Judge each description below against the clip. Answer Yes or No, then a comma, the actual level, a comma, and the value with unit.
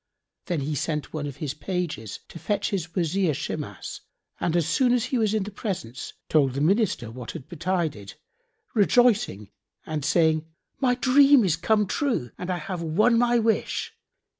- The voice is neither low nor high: Yes, medium, 175 Hz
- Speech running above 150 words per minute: Yes, average, 170 wpm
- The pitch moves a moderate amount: No, wide, 6.3 semitones